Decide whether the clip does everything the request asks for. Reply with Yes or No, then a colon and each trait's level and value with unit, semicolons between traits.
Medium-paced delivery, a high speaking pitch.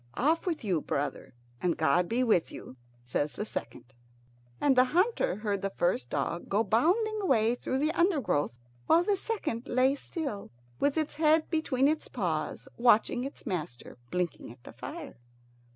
Yes: average, 165 wpm; high, 240 Hz